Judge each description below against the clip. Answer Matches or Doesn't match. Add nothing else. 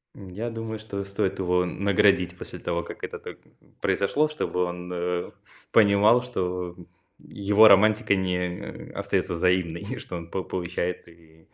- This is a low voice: Matches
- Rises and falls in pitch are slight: Matches